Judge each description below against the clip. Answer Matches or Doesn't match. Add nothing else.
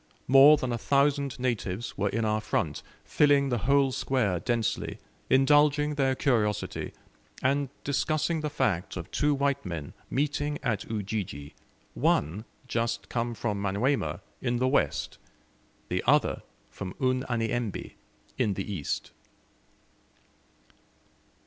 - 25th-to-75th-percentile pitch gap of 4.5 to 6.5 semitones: Matches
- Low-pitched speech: Matches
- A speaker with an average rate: Doesn't match